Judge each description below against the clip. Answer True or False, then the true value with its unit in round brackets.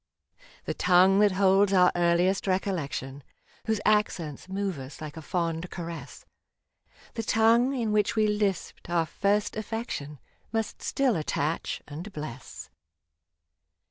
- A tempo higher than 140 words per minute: False (135 wpm)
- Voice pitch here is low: False (190 Hz)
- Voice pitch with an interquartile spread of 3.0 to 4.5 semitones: True (4.2 semitones)